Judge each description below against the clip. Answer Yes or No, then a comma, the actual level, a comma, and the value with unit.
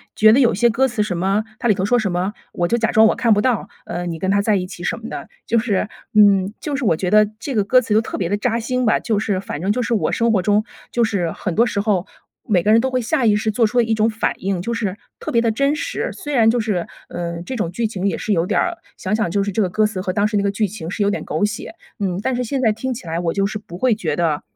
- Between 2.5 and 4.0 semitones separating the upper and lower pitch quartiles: Yes, average, 3.4 semitones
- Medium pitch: No, high, 210 Hz